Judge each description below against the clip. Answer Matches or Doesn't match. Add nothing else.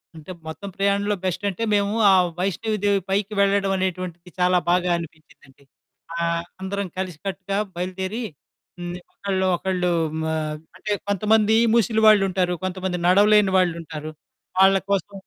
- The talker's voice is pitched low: Doesn't match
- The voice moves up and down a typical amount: Doesn't match